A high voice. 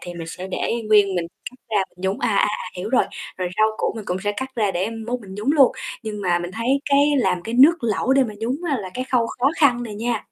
Yes: high, 215 Hz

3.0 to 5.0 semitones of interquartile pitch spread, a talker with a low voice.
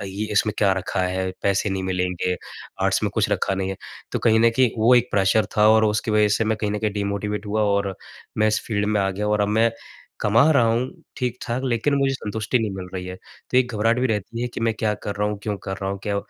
No: narrow, 2.6 semitones; low, 105 Hz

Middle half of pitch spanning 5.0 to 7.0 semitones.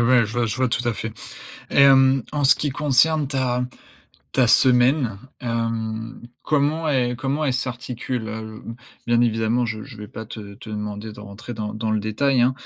No: average, 3.1 semitones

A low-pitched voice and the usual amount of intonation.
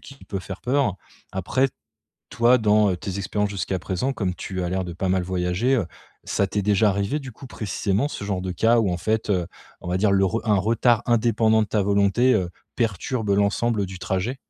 Yes: low, 100 Hz; average, 3.4 semitones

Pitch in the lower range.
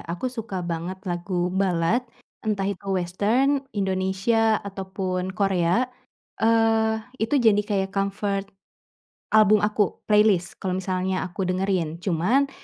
No: high, 195 Hz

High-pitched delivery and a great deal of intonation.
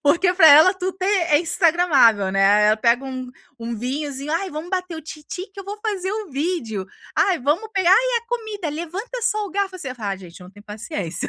Yes: very high, 325 Hz; wide, 8.1 semitones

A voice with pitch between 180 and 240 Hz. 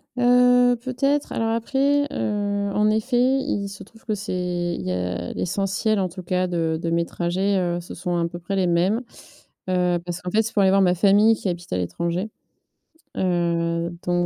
Yes: high, 190 Hz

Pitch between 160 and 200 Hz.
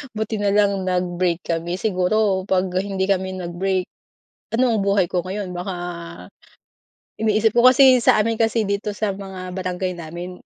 Yes: high, 190 Hz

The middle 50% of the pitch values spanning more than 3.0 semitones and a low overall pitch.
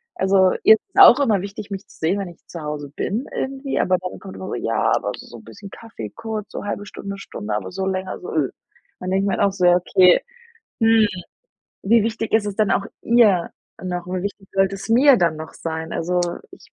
No: average, 3.4 semitones; high, 195 Hz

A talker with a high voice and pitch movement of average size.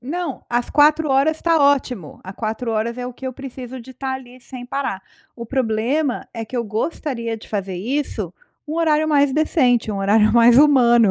Yes: very high, 250 Hz; average, 3.9 semitones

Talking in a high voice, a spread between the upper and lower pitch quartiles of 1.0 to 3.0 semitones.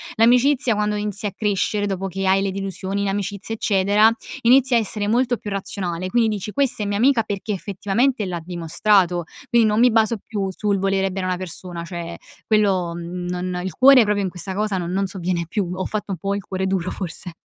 Yes: high, 195 Hz; narrow, 2.6 semitones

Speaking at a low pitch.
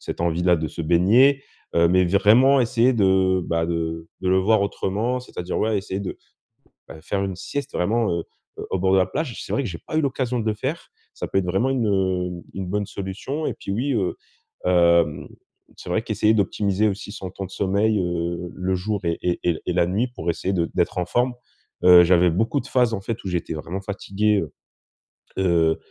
Yes: very low, 95 Hz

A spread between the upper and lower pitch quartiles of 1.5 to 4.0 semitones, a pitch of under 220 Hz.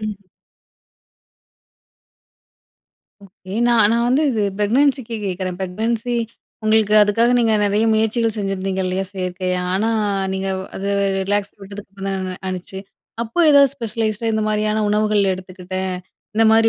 Yes: average, 2.8 semitones; high, 210 Hz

